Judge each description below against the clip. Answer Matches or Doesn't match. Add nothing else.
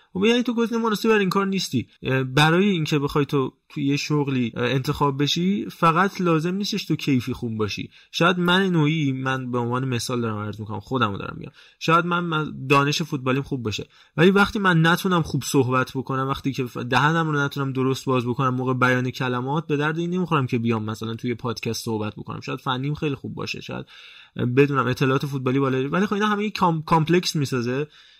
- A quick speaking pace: Matches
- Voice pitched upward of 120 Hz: Matches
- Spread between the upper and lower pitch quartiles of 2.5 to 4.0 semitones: Doesn't match